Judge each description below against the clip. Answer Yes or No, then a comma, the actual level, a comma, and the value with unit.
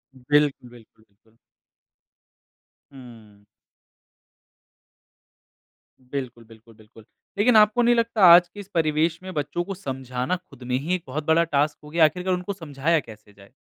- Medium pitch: Yes, medium, 150 Hz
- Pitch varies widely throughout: Yes, wide, 6.5 semitones